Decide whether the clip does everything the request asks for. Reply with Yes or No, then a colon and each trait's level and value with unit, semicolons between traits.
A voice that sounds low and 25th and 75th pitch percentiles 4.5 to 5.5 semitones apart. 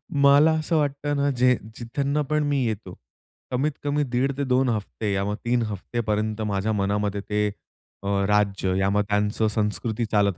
Yes: low, 115 Hz; average, 5.2 semitones